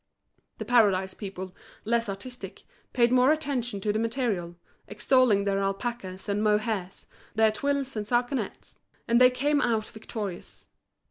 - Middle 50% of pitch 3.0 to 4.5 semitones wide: Yes, average, 3.8 semitones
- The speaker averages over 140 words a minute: No, slow, 135 wpm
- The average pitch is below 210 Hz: No, high, 220 Hz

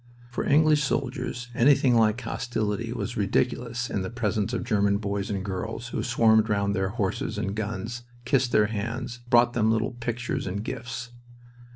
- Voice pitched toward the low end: Yes, low, 115 Hz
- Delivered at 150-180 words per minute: Yes, average, 165 wpm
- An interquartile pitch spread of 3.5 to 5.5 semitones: No, average, 2.9 semitones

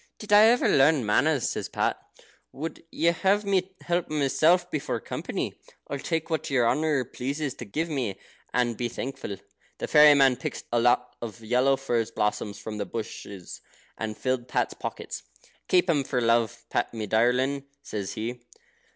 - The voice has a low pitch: Yes, low, 130 Hz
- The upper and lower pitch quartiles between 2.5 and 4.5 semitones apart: No, average, 5.0 semitones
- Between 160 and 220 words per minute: Yes, average, 170 wpm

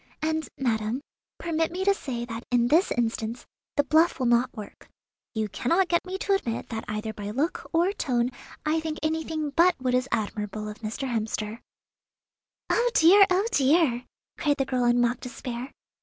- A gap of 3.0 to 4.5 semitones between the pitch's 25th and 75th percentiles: No, wide, 5.6 semitones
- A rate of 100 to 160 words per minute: No, average, 175 wpm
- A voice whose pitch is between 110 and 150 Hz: No, very high, 255 Hz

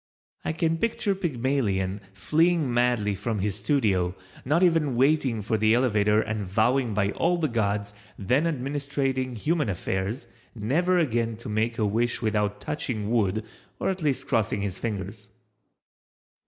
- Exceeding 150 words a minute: No, average, 145 wpm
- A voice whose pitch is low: Yes, low, 115 Hz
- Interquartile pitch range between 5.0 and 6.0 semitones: Yes, wide, 5.5 semitones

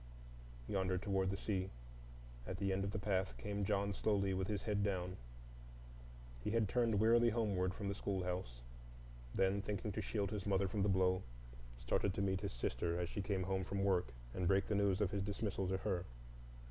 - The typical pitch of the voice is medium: No, low, 100 Hz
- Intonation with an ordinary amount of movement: No, narrow, 1.5 semitones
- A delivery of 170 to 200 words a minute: Yes, average, 190 wpm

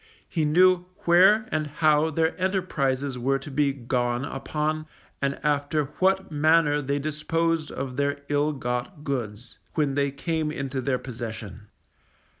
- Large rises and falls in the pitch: No, average, 3.0 semitones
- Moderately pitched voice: Yes, medium, 145 Hz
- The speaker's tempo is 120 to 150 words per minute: Yes, average, 140 wpm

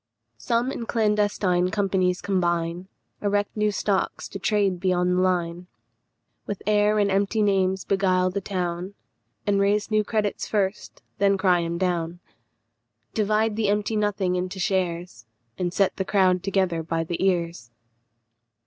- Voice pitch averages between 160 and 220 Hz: Yes, high, 190 Hz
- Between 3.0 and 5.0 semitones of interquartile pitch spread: No, narrow, 2.4 semitones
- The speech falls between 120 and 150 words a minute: Yes, average, 140 wpm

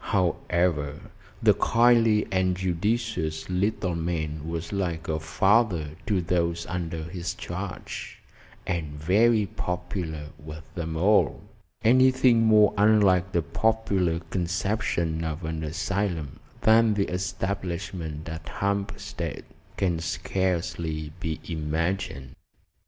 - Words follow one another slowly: Yes, slow, 105 wpm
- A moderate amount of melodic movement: Yes, average, 3.7 semitones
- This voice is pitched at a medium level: No, very low, 90 Hz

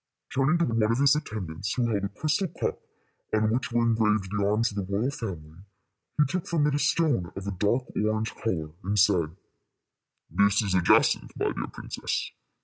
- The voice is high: No, low, 110 Hz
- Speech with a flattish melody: No, average, 4.5 semitones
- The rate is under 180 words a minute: No, average, 195 wpm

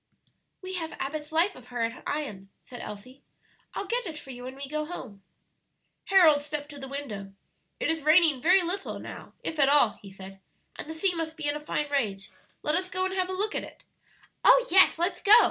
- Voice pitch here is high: Yes, very high, 300 Hz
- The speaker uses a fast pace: Yes, fast, 220 wpm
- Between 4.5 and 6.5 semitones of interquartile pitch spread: Yes, wide, 5.6 semitones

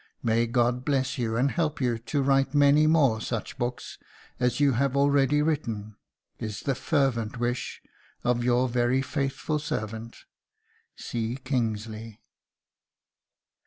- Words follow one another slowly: Yes, slow, 125 wpm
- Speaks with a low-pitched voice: Yes, low, 125 Hz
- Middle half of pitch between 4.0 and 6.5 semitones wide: No, average, 3.2 semitones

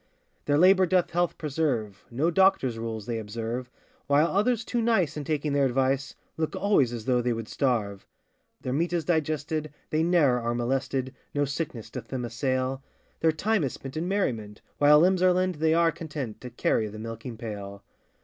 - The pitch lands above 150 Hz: No, medium, 140 Hz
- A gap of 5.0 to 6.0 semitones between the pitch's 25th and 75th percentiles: Yes, wide, 5.6 semitones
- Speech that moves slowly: No, average, 185 wpm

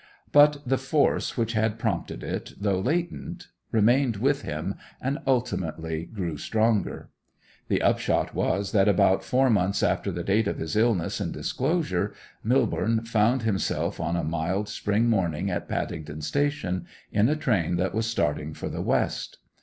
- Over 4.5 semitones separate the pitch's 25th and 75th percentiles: Yes, wide, 5.5 semitones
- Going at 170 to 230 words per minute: No, average, 155 wpm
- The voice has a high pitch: No, low, 110 Hz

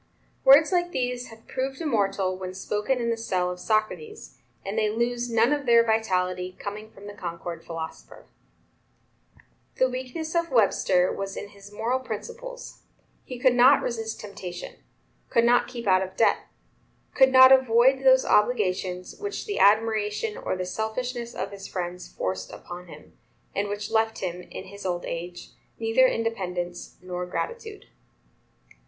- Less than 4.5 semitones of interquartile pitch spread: No, average, 5.3 semitones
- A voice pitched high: Yes, high, 220 Hz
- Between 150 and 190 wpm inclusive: Yes, average, 155 wpm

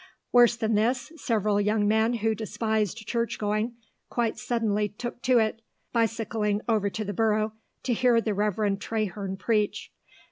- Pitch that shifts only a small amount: Yes, narrow, 1.7 semitones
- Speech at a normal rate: Yes, average, 150 wpm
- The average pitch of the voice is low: No, high, 220 Hz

